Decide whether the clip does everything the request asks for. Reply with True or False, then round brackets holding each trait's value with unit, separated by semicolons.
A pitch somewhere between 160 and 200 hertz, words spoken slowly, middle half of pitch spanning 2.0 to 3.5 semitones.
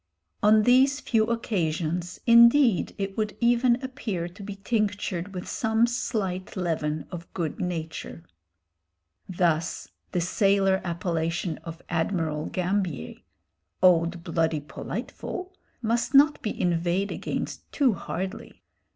False (190 Hz; 115 wpm; 4.7 semitones)